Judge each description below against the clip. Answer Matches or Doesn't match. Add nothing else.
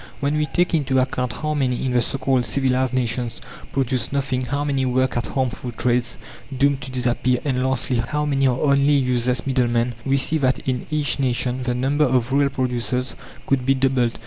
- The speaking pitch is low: Matches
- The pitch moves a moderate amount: Doesn't match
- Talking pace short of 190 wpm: Doesn't match